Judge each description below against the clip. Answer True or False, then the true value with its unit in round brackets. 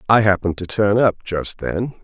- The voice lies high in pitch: False (100 Hz)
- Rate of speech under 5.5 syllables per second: True (5.3 syllables/s)